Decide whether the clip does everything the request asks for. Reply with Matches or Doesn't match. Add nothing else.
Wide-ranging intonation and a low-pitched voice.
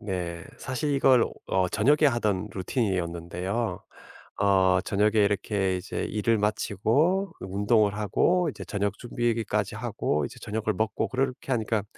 Doesn't match